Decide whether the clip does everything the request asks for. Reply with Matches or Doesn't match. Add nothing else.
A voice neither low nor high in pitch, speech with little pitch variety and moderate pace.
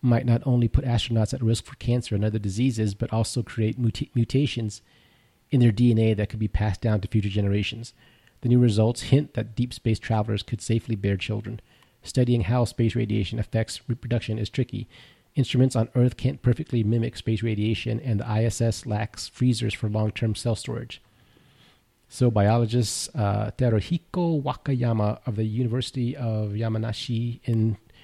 Doesn't match